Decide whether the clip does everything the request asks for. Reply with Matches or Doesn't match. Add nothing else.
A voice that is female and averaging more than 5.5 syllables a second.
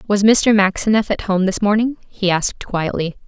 Doesn't match